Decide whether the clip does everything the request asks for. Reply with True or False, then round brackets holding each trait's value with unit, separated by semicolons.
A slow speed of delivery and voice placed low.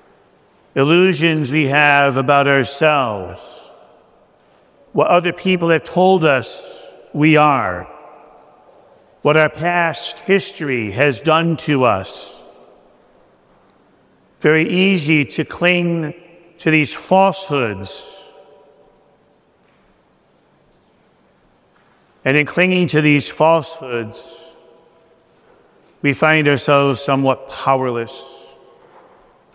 False (80 wpm; 155 Hz)